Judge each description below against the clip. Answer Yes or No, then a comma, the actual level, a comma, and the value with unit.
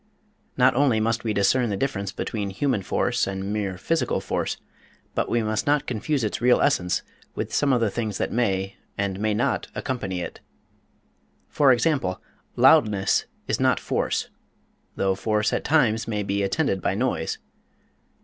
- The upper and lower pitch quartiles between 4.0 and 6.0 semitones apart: Yes, average, 4.3 semitones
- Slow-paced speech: No, average, 160 wpm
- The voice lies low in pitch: Yes, low, 110 Hz